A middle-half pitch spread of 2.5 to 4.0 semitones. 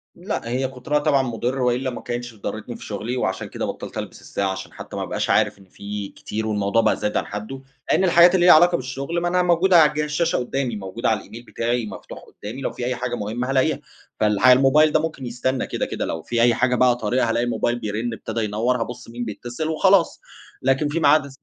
No: average, 4.5 semitones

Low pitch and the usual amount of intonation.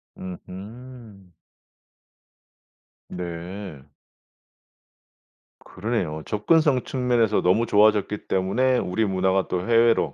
Yes: low, 105 Hz; average, 4.2 semitones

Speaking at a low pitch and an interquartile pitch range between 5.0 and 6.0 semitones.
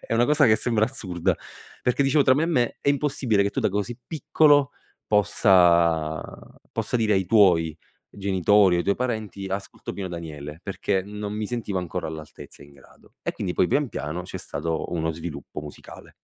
Yes: low, 100 Hz; wide, 5.6 semitones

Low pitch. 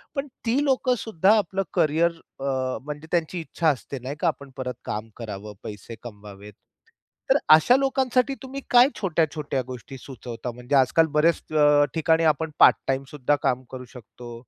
No: medium, 145 Hz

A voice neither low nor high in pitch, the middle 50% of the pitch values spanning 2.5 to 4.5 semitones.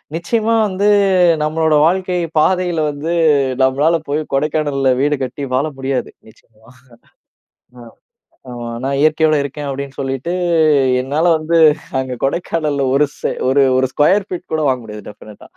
Yes: medium, 145 Hz; average, 3.8 semitones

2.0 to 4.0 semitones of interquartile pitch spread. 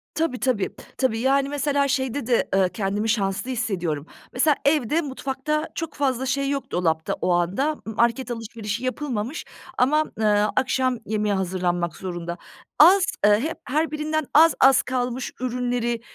No: average, 5.1 semitones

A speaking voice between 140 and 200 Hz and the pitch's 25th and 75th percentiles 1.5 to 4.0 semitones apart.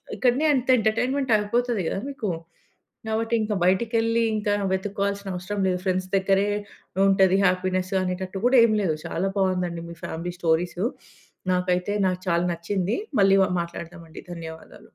Yes: high, 190 Hz; average, 2.9 semitones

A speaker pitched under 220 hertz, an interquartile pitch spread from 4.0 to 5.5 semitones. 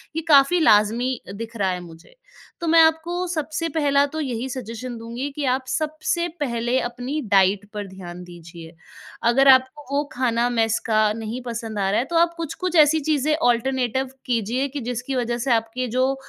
No: very high, 250 Hz; average, 4.4 semitones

